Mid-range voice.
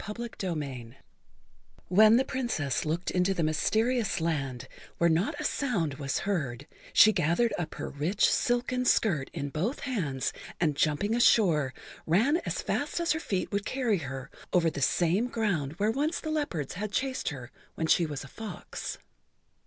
Yes: medium, 180 Hz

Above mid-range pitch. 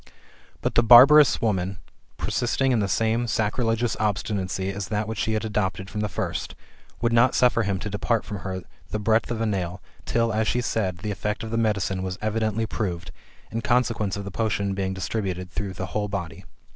No: low, 105 Hz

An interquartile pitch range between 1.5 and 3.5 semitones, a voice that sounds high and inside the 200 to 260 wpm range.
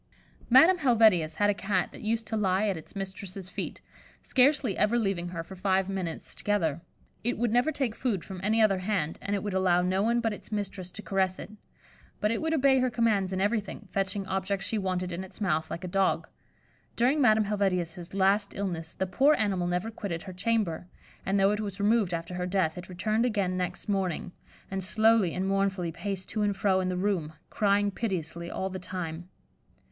Yes: average, 2.8 semitones; high, 195 Hz; fast, 205 wpm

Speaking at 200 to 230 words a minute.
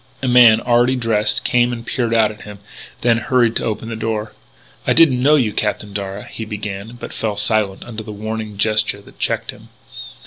Yes: fast, 205 wpm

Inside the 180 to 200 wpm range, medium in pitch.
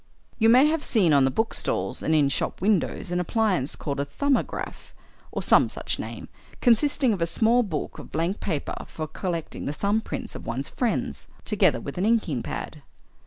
Yes: average, 185 wpm; medium, 180 Hz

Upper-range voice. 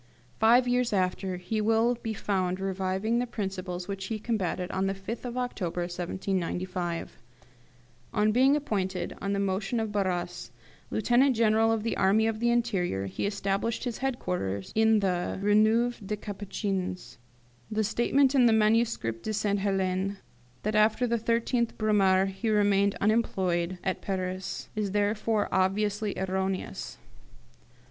Yes: high, 205 Hz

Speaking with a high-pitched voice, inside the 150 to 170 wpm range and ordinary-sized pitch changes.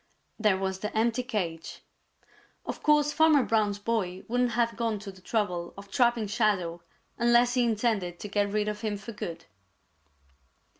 Yes: high, 215 Hz; average, 160 wpm; average, 3.2 semitones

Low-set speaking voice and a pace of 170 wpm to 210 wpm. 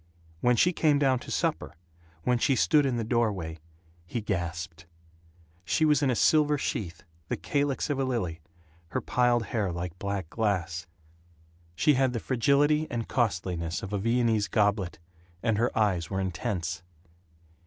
No: low, 110 Hz; average, 155 wpm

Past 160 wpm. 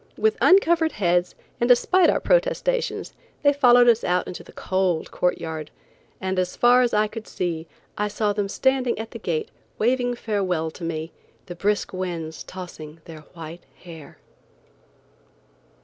No: average, 155 wpm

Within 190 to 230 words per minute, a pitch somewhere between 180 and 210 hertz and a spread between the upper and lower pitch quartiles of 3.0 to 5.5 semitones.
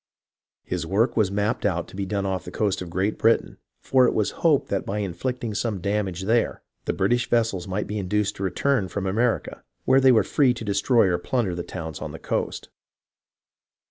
No: fast, 205 wpm; low, 100 Hz; average, 3.6 semitones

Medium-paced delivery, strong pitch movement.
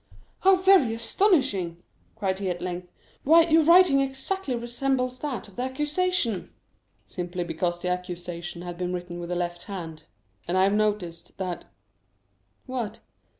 Yes: average, 150 wpm; wide, 7.4 semitones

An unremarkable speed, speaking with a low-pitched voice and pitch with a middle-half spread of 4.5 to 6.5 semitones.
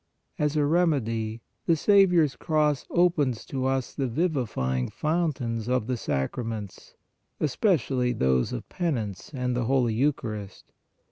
No: slow, 130 wpm; low, 130 Hz; average, 5.3 semitones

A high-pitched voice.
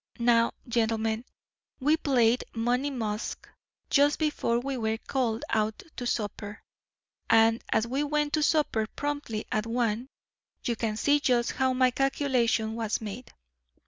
Yes: high, 235 Hz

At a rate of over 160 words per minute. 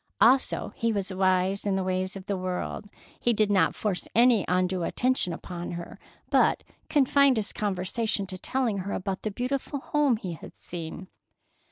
Yes: average, 170 wpm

